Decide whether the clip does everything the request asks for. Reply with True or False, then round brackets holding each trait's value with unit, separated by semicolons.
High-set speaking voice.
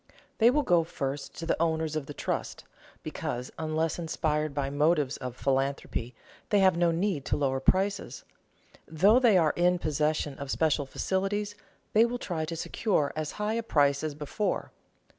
False (160 Hz)